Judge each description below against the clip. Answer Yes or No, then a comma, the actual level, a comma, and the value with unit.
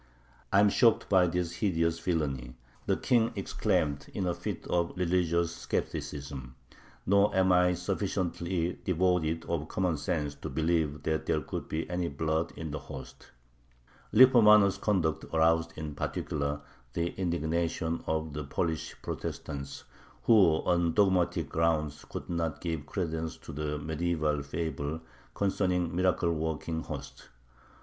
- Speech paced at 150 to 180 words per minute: No, slow, 135 wpm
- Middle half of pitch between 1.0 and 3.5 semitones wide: Yes, narrow, 2.5 semitones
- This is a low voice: Yes, very low, 85 Hz